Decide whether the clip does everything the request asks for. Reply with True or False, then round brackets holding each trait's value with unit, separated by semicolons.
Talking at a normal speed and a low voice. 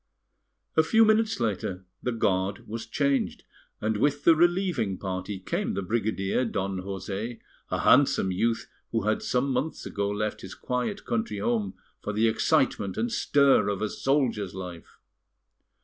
True (150 wpm; 115 Hz)